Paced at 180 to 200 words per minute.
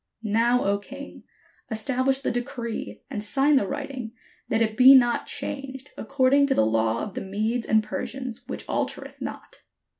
No: average, 160 wpm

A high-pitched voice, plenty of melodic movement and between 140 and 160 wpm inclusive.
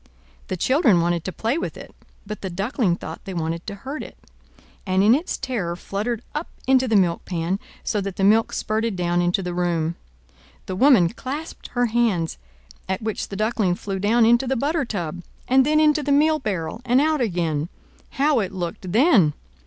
No: high, 210 Hz; wide, 6.4 semitones; average, 190 wpm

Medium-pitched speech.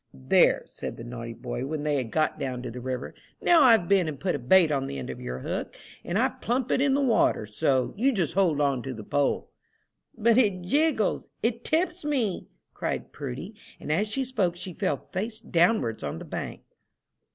Yes: medium, 175 Hz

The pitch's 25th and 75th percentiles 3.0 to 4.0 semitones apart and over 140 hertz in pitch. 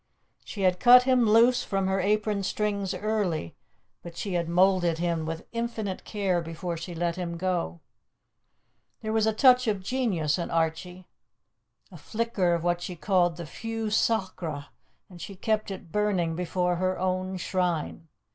Yes: average, 3.6 semitones; medium, 185 Hz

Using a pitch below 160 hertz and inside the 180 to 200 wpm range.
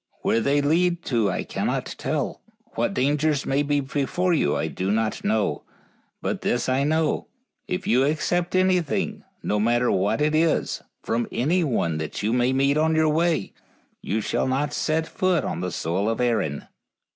No: medium, 140 Hz; average, 170 wpm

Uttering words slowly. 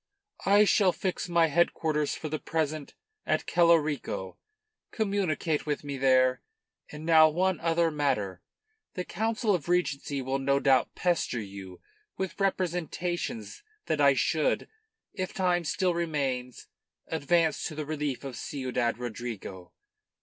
Yes: slow, 130 wpm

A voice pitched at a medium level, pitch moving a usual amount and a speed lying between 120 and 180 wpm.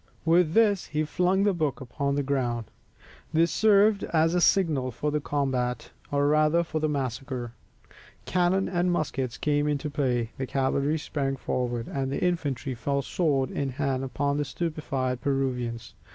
Yes: medium, 145 Hz; average, 3.7 semitones; average, 160 wpm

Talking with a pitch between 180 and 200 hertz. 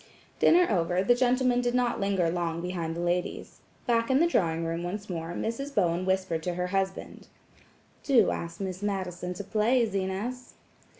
Yes: high, 190 Hz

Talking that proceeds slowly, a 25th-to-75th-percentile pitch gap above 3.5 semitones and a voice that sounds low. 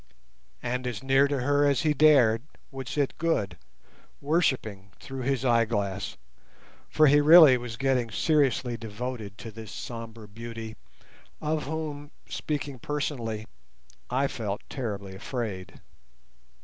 Yes: slow, 125 wpm; average, 4.2 semitones; low, 125 Hz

